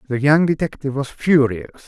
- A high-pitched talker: No, medium, 140 Hz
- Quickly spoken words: No, average, 160 wpm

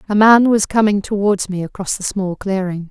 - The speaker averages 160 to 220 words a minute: Yes, fast, 205 wpm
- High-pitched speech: Yes, high, 200 Hz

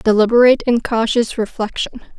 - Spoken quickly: No, slow, 110 wpm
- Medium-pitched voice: No, high, 230 Hz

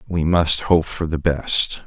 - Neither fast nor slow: Yes, average, 195 wpm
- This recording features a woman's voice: No, male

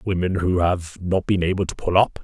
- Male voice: Yes, male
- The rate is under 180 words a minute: No, fast, 240 wpm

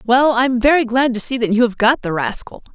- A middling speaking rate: No, fast, 260 wpm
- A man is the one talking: No, female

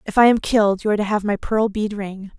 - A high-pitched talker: Yes, high, 210 Hz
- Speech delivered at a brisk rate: Yes, fast, 300 wpm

